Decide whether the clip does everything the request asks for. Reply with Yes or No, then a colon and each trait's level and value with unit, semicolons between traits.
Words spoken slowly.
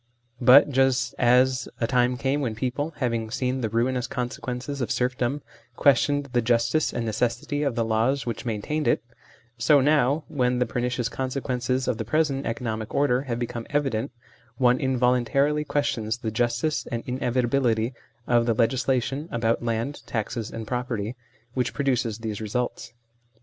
No: average, 155 wpm